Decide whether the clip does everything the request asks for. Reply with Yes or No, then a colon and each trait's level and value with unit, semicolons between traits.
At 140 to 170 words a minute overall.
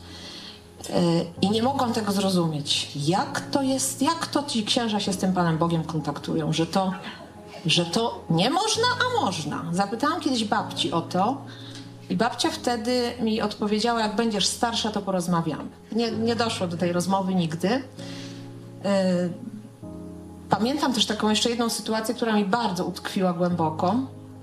Yes: average, 145 wpm